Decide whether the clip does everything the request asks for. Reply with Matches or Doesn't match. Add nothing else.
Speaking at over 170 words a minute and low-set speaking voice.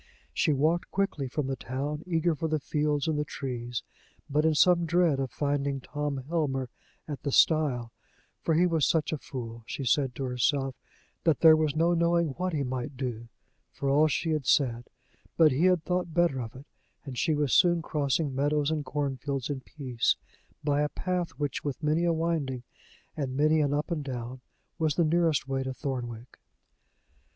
Doesn't match